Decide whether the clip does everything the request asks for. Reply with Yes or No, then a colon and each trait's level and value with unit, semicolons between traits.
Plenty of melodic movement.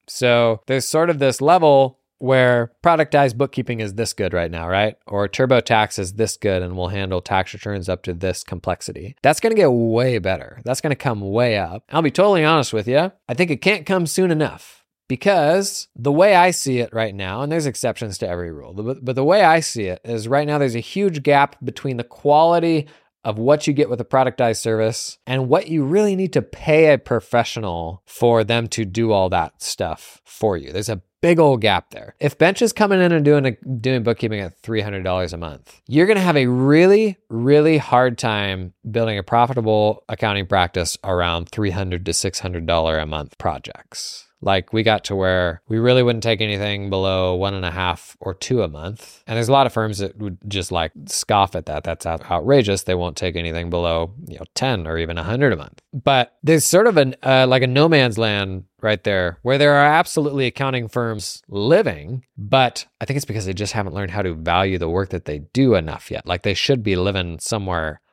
Yes: wide, 6.4 semitones